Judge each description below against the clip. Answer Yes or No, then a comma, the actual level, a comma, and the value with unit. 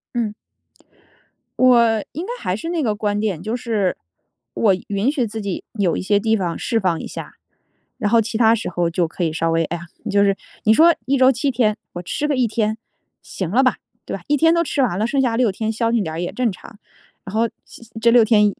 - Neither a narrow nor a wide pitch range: Yes, average, 3.8 semitones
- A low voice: No, high, 220 Hz